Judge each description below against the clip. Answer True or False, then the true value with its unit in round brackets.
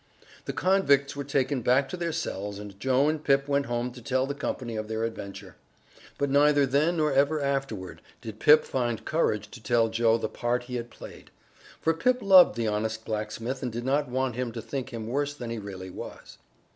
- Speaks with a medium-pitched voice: False (125 Hz)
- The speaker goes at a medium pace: False (210 wpm)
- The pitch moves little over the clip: False (4.1 semitones)